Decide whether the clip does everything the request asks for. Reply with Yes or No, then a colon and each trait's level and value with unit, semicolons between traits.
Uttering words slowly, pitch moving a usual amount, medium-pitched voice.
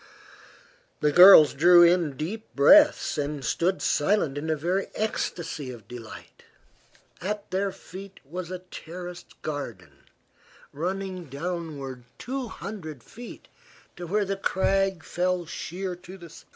Yes: slow, 130 wpm; average, 4.4 semitones; medium, 175 Hz